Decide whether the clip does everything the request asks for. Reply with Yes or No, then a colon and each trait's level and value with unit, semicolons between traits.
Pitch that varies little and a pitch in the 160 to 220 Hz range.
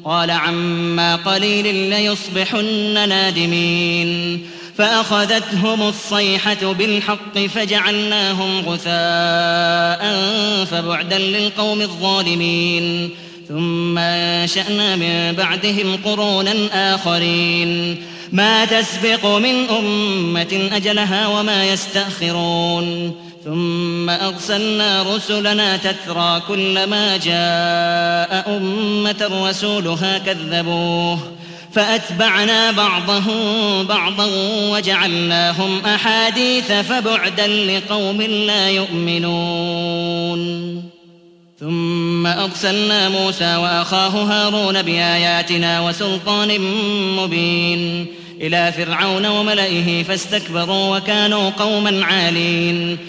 No: average, 3.3 semitones; high, 190 Hz